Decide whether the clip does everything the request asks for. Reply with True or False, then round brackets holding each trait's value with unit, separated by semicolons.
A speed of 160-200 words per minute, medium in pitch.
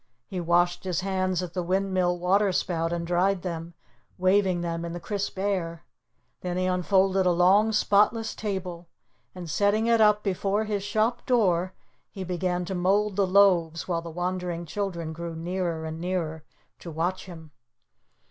True (165 wpm; 180 Hz)